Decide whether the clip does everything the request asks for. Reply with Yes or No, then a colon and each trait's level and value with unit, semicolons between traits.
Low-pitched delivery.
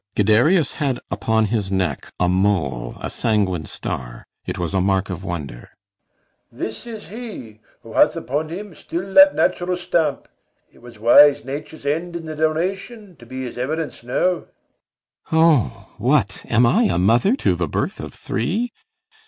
Yes: low, 130 Hz